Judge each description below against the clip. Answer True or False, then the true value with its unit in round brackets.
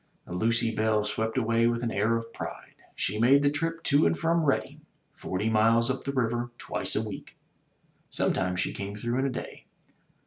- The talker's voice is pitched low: True (115 Hz)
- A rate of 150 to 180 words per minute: False (195 wpm)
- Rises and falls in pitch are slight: False (3.3 semitones)